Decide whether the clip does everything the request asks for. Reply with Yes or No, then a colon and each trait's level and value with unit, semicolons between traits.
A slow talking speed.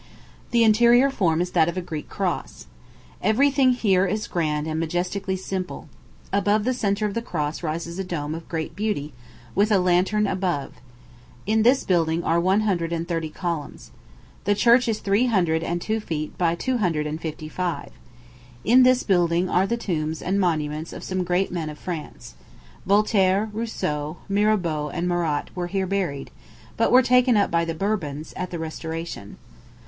No: average, 180 wpm